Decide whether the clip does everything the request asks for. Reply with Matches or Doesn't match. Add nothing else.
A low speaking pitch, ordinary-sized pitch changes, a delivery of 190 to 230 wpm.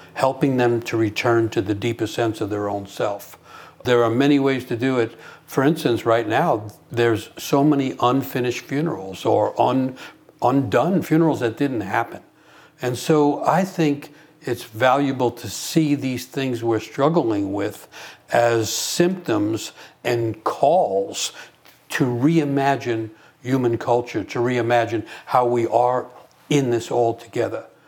Doesn't match